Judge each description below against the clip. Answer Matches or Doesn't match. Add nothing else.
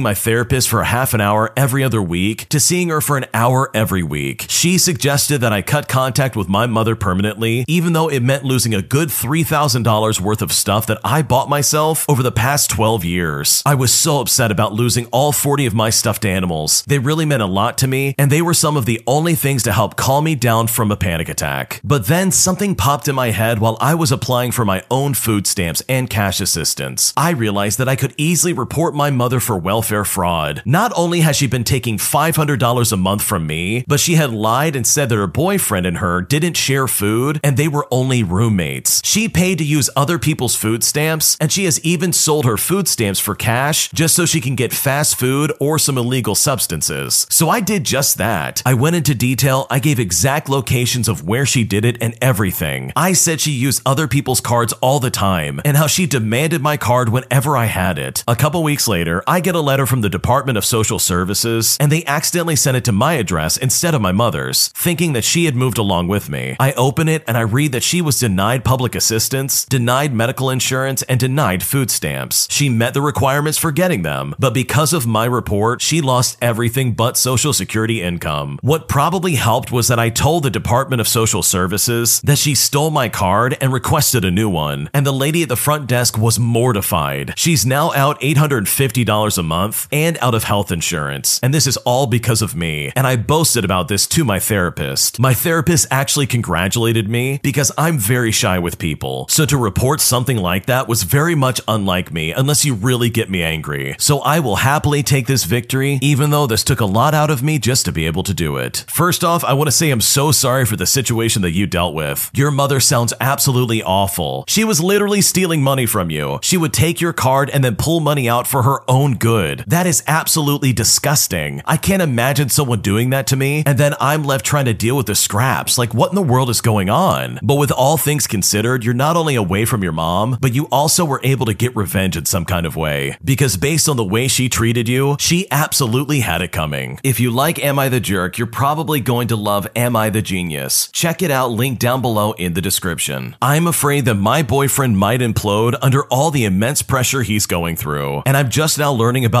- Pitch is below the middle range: Matches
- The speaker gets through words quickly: Matches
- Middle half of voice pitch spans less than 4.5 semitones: Doesn't match